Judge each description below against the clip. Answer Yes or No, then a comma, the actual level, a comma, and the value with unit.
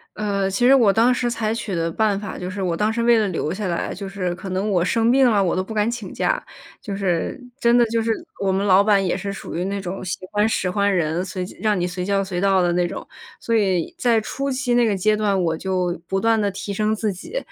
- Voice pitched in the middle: No, high, 200 Hz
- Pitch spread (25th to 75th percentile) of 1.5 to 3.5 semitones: Yes, average, 3.1 semitones